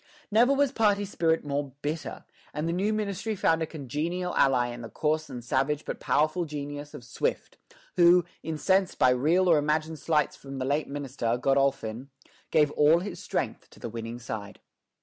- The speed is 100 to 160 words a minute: No, average, 175 wpm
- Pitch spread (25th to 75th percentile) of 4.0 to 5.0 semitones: Yes, average, 4.3 semitones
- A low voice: No, medium, 150 Hz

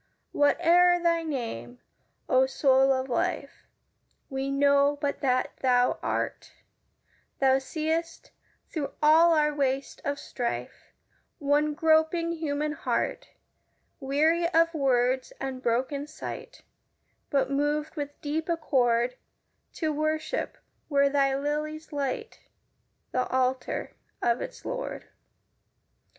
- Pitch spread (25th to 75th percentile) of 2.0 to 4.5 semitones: Yes, average, 3.0 semitones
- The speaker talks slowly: Yes, slow, 110 wpm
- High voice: Yes, very high, 285 Hz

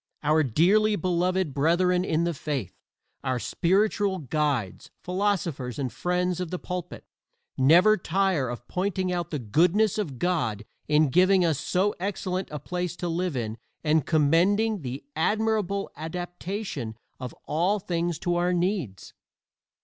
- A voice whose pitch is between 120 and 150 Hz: No, medium, 175 Hz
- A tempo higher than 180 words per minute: No, average, 140 wpm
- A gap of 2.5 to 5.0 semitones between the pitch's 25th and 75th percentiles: Yes, average, 3.9 semitones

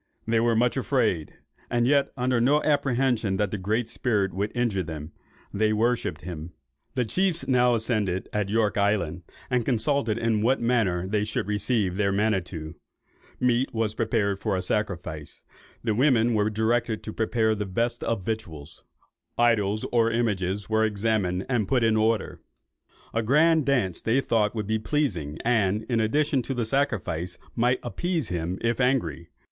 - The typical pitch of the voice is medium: No, low, 110 Hz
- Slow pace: No, average, 165 wpm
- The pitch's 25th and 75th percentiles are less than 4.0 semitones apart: Yes, average, 3.5 semitones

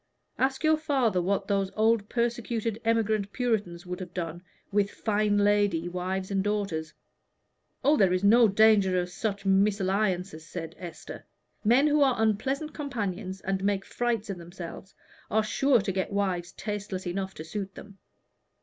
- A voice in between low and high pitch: No, high, 200 Hz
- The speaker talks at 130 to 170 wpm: Yes, average, 155 wpm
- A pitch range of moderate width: Yes, average, 3.2 semitones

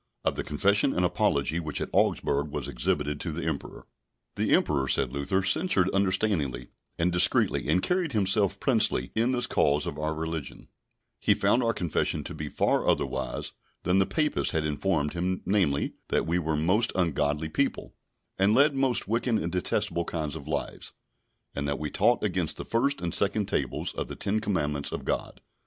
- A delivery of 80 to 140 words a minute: No, average, 175 wpm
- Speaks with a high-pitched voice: No, very low, 85 Hz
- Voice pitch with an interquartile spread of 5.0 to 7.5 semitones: Yes, wide, 5.6 semitones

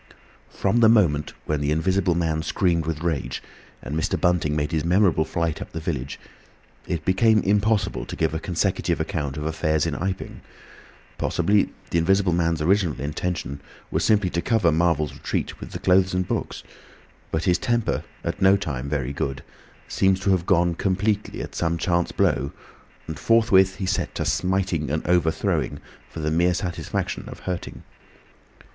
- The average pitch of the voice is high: No, very low, 85 Hz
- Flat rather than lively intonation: No, average, 3.5 semitones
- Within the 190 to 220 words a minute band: No, average, 165 wpm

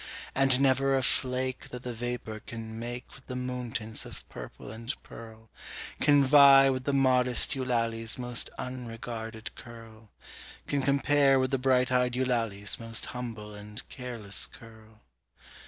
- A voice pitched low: Yes, low, 125 Hz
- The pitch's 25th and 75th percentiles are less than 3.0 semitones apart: Yes, narrow, 2.4 semitones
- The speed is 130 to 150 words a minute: Yes, average, 145 wpm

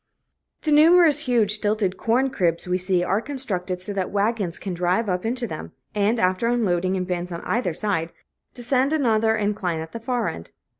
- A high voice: Yes, high, 205 Hz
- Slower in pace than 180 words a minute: No, average, 185 wpm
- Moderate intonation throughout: Yes, average, 4.8 semitones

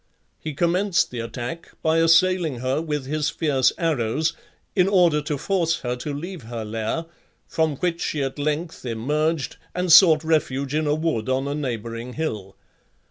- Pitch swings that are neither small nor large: Yes, average, 4.2 semitones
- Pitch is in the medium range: Yes, medium, 150 Hz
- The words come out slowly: No, average, 165 wpm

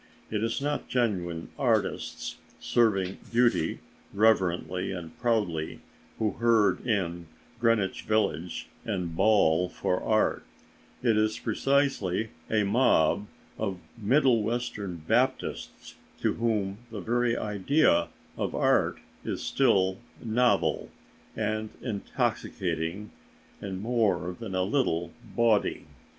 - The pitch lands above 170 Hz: No, low, 105 Hz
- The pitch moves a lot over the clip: No, average, 4.2 semitones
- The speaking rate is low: Yes, slow, 105 wpm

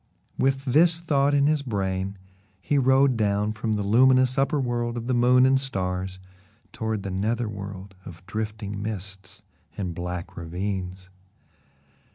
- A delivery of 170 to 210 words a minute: No, average, 145 wpm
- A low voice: Yes, low, 110 Hz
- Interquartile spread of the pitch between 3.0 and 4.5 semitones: No, average, 5.3 semitones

